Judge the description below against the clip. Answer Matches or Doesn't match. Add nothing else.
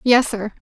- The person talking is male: Doesn't match